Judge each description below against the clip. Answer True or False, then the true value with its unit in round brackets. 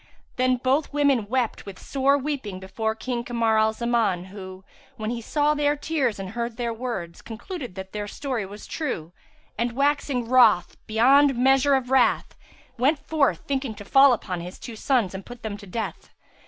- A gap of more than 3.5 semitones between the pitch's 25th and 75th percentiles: True (4.4 semitones)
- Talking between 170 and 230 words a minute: True (180 wpm)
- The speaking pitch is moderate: False (240 Hz)